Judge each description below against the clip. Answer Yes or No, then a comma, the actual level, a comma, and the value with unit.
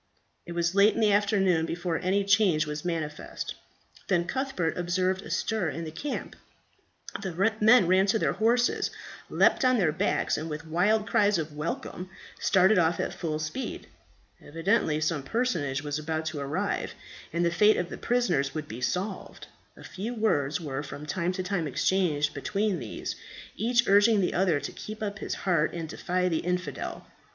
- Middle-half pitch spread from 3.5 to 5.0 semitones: Yes, average, 4.5 semitones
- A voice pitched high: No, medium, 180 Hz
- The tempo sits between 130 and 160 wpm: No, average, 175 wpm